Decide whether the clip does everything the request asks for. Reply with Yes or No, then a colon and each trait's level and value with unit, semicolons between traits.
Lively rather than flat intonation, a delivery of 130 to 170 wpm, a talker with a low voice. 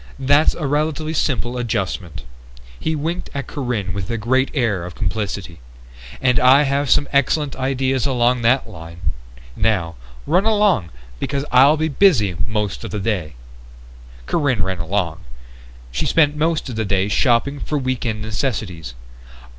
Yes: wide, 6.0 semitones; average, 150 wpm; low, 125 Hz